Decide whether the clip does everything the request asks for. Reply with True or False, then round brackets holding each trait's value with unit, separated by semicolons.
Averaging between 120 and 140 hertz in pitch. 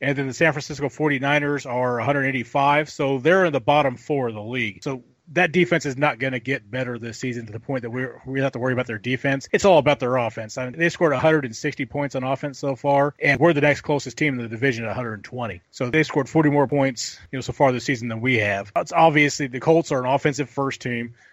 True (135 Hz)